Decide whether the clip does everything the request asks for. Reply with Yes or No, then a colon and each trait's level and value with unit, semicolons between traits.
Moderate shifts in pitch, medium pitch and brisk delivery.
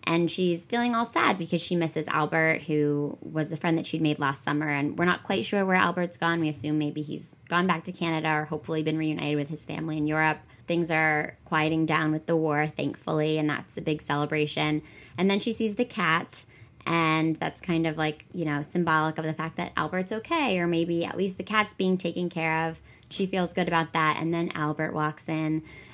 No: narrow, 2.2 semitones; medium, 160 Hz; fast, 220 wpm